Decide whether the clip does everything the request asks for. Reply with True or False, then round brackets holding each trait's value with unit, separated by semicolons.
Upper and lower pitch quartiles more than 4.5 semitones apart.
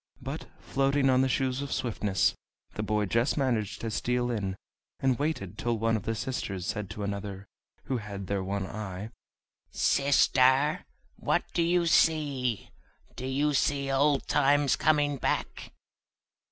True (5.0 semitones)